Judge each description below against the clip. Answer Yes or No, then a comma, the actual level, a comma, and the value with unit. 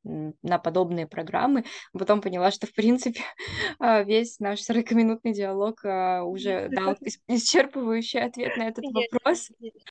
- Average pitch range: Yes, average, 3.6 semitones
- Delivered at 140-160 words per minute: No, average, 115 wpm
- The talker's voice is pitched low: No, high, 225 Hz